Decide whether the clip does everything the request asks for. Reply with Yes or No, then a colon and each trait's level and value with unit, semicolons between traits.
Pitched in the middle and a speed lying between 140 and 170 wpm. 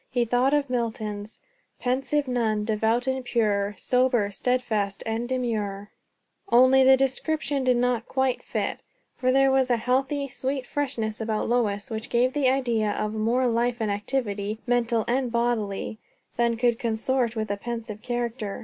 No: high, 240 Hz; average, 155 wpm